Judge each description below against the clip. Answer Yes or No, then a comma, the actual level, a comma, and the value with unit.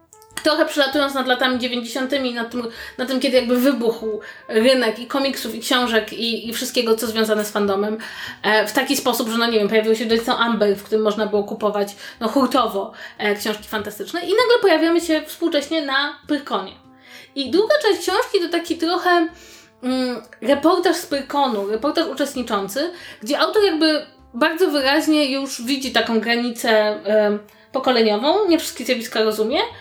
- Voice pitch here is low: No, very high, 255 Hz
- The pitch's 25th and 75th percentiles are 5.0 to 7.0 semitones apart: Yes, wide, 5.6 semitones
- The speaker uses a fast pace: Yes, fast, 165 wpm